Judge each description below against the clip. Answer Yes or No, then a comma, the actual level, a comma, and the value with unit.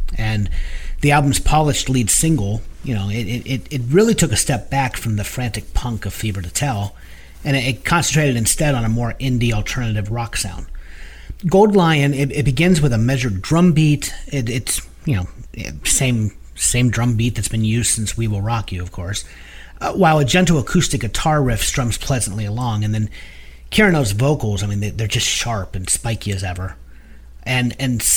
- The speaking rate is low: No, average, 195 wpm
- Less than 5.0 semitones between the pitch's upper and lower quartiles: No, wide, 5.5 semitones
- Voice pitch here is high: No, low, 115 Hz